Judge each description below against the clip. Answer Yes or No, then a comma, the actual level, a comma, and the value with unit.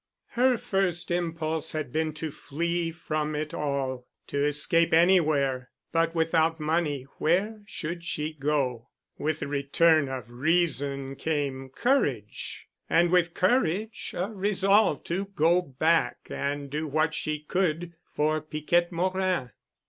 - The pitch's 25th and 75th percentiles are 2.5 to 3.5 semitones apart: Yes, average, 3.1 semitones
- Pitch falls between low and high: Yes, medium, 160 Hz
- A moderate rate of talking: No, slow, 125 wpm